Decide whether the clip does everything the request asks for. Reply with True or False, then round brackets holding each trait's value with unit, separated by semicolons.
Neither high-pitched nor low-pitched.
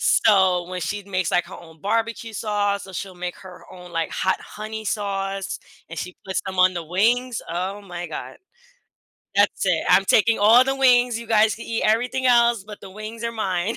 False (200 Hz)